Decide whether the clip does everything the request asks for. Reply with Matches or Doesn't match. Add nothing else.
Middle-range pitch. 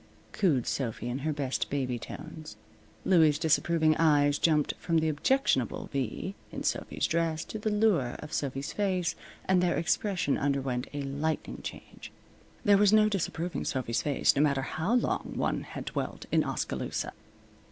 Matches